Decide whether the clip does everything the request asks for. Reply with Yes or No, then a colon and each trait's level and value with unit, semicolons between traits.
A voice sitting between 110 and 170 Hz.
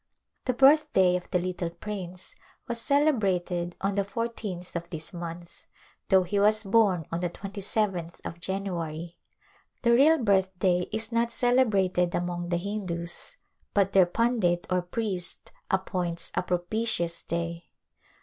No: medium, 185 Hz